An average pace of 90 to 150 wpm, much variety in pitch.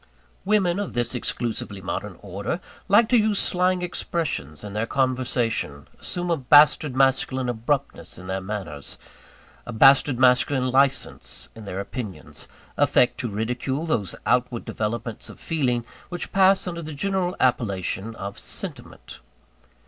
Yes: slow, 135 wpm; wide, 7.0 semitones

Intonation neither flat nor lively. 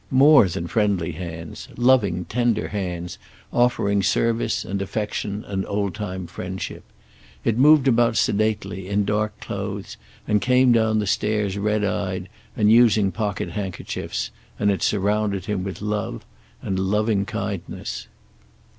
No: narrow, 2.2 semitones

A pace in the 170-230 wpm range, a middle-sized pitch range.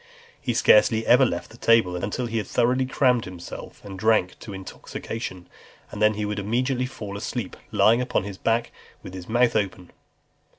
Yes: average, 175 wpm; average, 3.7 semitones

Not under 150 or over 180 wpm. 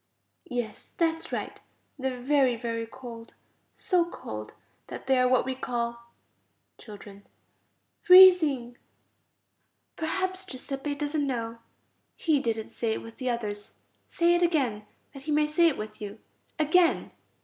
No: average, 140 wpm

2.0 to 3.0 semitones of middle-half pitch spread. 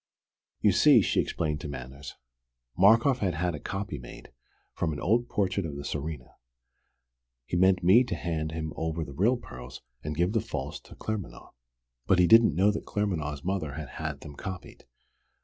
No: average, 4.8 semitones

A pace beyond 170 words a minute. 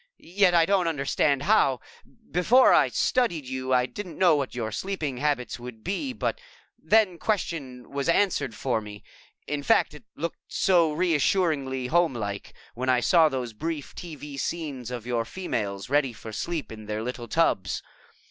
No: average, 160 wpm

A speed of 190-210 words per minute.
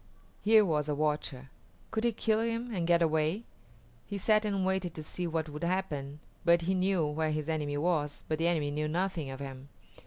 Yes: fast, 205 wpm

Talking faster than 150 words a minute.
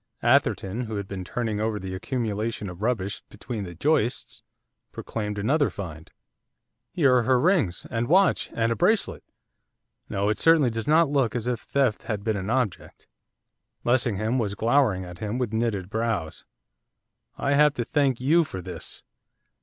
Yes: average, 160 wpm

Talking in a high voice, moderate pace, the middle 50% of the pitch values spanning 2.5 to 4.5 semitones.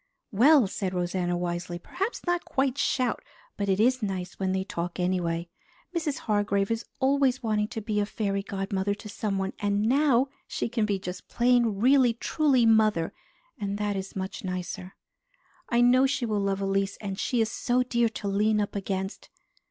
Yes: high, 205 Hz; average, 175 wpm; average, 4.0 semitones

